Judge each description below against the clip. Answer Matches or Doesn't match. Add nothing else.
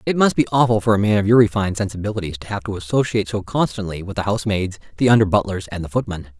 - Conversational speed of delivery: Doesn't match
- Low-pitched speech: Matches